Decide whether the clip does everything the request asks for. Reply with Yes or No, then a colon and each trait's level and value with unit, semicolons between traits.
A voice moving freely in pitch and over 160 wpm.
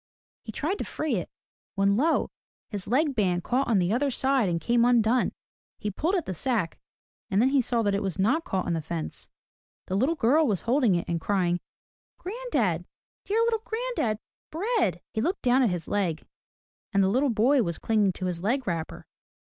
Yes: wide, 6.7 semitones; average, 200 wpm